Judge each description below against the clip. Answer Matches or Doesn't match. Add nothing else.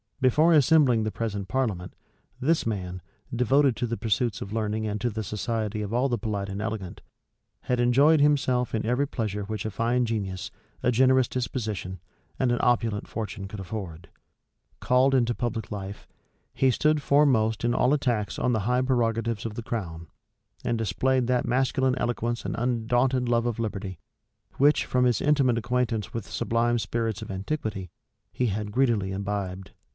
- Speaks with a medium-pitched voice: Doesn't match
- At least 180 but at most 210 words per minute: Doesn't match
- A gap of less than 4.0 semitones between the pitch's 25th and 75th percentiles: Matches